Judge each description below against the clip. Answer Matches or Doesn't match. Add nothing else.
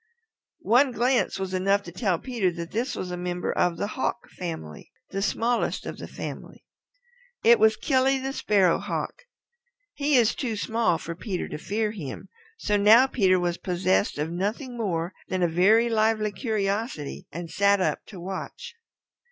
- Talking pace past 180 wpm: Doesn't match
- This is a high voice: Matches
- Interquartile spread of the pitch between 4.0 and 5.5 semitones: Matches